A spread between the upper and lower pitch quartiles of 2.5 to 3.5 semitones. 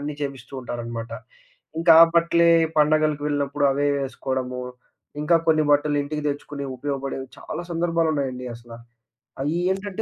Yes: average, 2.8 semitones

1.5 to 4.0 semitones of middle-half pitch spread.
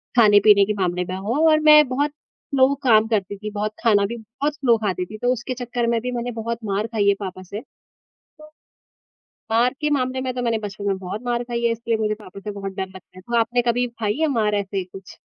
Yes: average, 3.5 semitones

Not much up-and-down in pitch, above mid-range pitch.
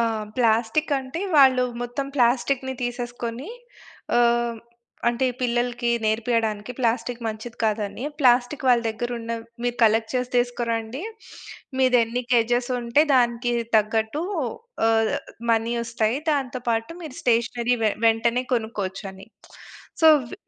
Yes: narrow, 1.7 semitones; high, 240 Hz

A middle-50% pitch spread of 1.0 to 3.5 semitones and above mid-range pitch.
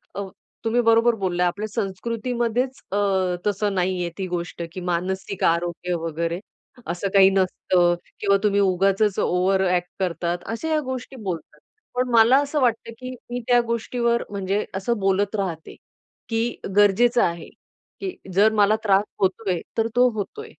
No: average, 4.3 semitones; high, 200 Hz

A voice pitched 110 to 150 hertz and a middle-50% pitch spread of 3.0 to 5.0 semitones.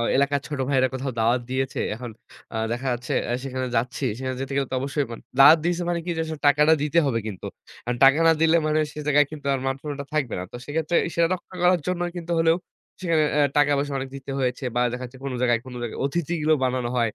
Yes: medium, 140 Hz; average, 3.5 semitones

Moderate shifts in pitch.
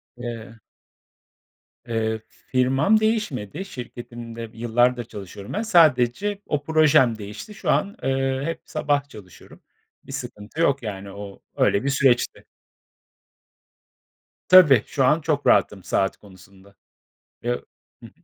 No: wide, 5.9 semitones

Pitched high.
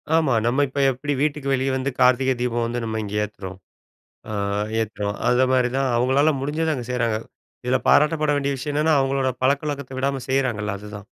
No: low, 130 Hz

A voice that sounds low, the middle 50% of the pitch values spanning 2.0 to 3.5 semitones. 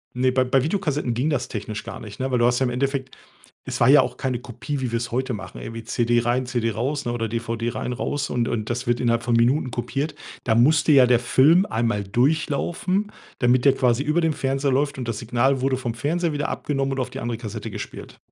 Yes: low, 125 Hz; average, 2.8 semitones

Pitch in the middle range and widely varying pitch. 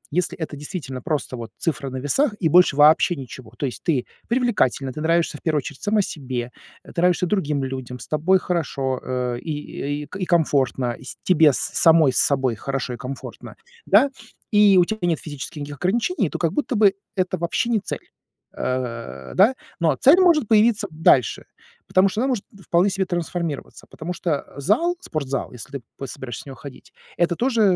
Yes: medium, 160 Hz; wide, 6.0 semitones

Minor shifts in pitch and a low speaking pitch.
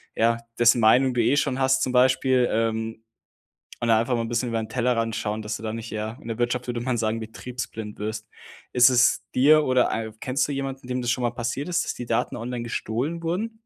Yes: narrow, 2.3 semitones; low, 120 Hz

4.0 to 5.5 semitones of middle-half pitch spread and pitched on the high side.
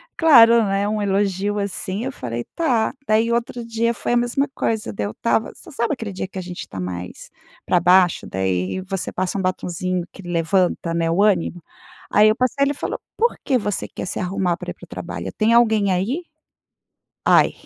Yes: average, 4.6 semitones; high, 200 Hz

